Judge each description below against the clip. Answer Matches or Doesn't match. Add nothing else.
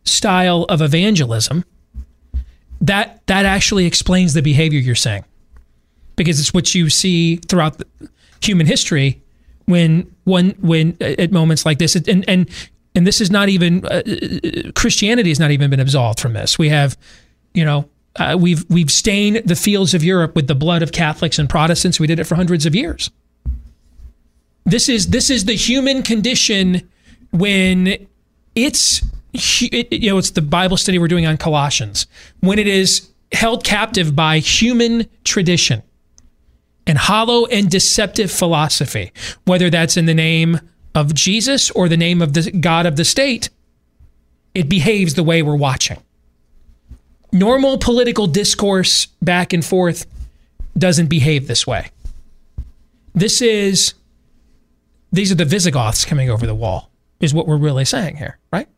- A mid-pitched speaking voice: Matches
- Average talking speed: Matches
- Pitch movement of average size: Doesn't match